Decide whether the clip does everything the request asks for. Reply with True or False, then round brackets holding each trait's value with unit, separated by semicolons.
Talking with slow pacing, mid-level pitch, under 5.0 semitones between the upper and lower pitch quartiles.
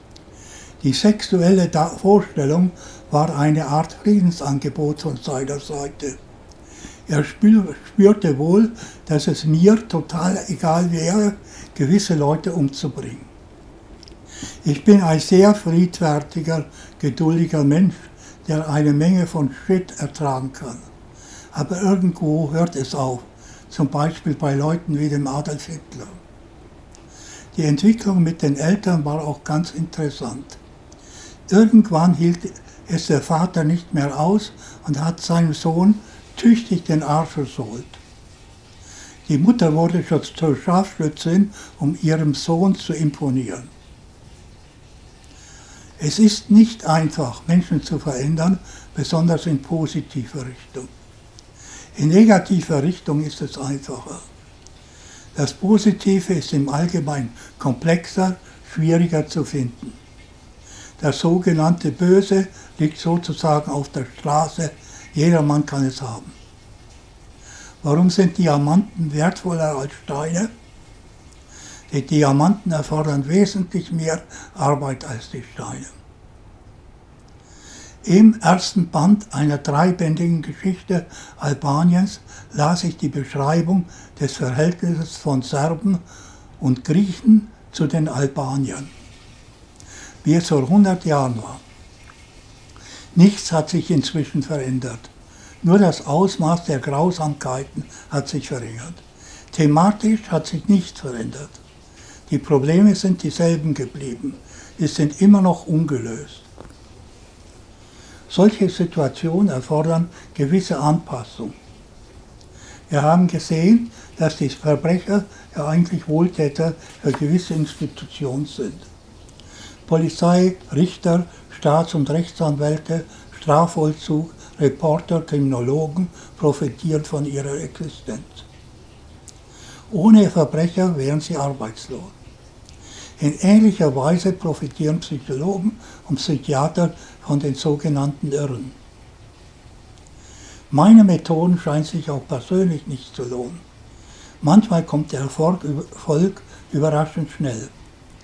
True (100 wpm; 155 Hz; 3.8 semitones)